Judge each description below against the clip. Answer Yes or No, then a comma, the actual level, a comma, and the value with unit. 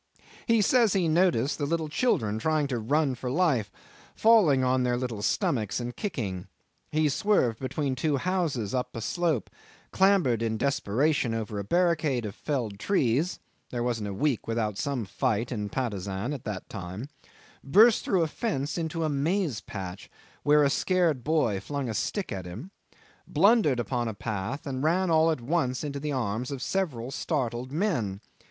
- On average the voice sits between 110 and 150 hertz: Yes, low, 135 Hz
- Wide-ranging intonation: Yes, wide, 6.0 semitones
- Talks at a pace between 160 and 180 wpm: Yes, average, 170 wpm